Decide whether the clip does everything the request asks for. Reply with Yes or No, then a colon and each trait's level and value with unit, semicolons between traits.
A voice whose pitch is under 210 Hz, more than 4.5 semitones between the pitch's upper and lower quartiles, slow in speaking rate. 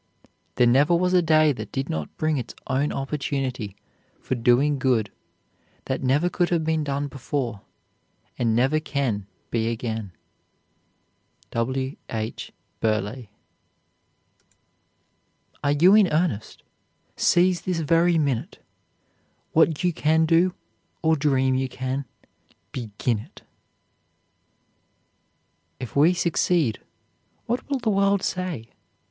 Yes: medium, 140 Hz; average, 5.3 semitones; slow, 115 wpm